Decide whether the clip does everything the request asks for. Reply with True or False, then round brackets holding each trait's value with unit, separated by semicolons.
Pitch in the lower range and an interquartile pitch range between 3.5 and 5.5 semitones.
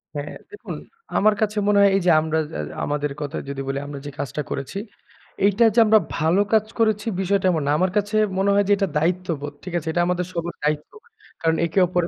False (175 Hz; 5.0 semitones)